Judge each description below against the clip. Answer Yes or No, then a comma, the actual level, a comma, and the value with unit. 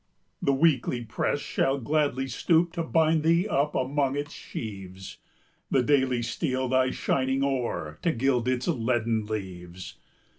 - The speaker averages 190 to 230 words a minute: No, average, 140 wpm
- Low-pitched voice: Yes, low, 130 Hz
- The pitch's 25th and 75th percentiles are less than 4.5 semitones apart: Yes, average, 3.9 semitones